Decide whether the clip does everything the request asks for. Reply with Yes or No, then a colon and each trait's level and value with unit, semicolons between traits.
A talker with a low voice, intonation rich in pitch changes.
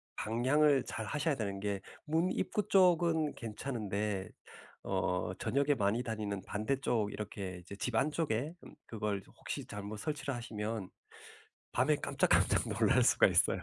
Yes: low, 110 Hz; wide, 5.9 semitones